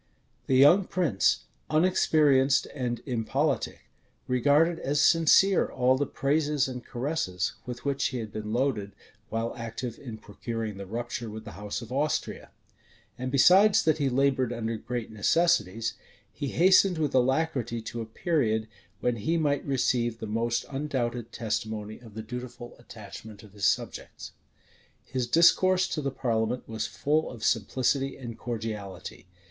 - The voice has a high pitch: No, low, 125 Hz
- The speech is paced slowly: No, average, 145 wpm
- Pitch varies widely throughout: No, average, 4.3 semitones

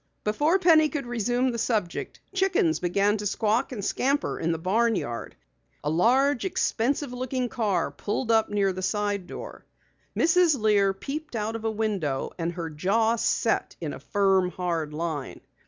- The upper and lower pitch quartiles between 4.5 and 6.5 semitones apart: Yes, wide, 5.4 semitones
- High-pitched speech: Yes, high, 215 Hz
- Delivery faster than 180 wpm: No, average, 165 wpm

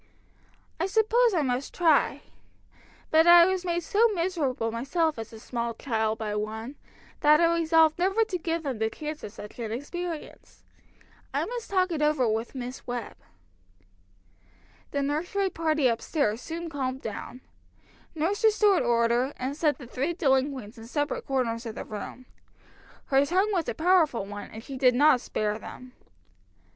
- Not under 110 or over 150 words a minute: No, average, 165 wpm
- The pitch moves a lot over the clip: Yes, wide, 6.3 semitones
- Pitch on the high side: Yes, very high, 285 Hz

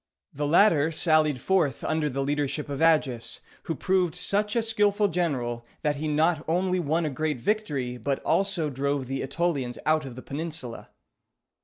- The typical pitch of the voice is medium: Yes, medium, 155 Hz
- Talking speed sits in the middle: Yes, average, 165 wpm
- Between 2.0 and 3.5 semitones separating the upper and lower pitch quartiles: No, average, 4.3 semitones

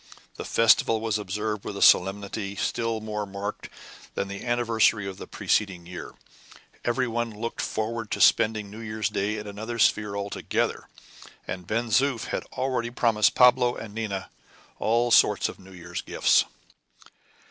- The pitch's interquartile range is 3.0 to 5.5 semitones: No, narrow, 2.5 semitones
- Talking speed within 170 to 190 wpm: No, average, 155 wpm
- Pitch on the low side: Yes, low, 110 Hz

